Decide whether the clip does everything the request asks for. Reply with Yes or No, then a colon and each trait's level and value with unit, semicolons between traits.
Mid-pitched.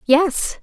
No: very high, 310 Hz